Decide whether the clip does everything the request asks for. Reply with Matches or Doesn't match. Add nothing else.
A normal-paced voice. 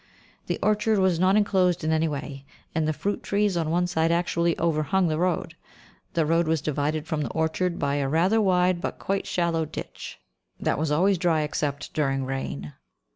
Matches